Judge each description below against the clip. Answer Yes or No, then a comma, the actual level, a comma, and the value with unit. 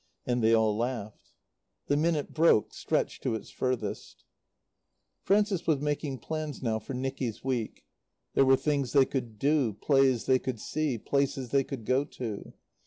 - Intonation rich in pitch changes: No, average, 3.8 semitones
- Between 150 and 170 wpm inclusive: Yes, average, 160 wpm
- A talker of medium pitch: No, low, 130 Hz